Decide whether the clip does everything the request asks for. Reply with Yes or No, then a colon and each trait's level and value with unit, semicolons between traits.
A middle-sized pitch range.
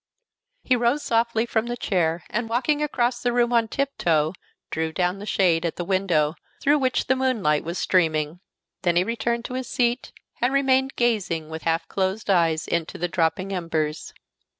No: wide, 6.5 semitones